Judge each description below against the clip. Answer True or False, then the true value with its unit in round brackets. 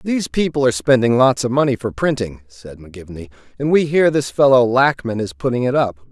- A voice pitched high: False (125 Hz)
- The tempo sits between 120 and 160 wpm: False (205 wpm)